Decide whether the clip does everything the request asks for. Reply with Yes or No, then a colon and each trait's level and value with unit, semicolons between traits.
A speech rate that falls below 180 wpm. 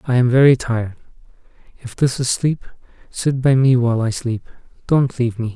No: average, 185 wpm